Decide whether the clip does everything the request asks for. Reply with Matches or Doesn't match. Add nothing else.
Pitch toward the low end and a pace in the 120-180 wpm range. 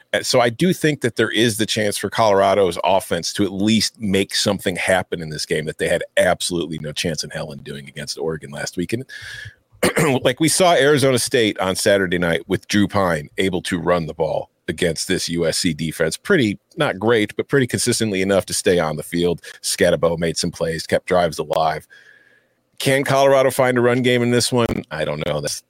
Doesn't match